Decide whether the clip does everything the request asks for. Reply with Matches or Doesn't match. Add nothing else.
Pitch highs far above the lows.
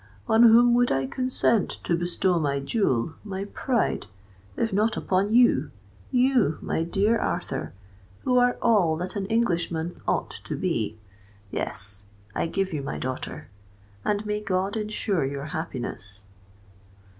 Matches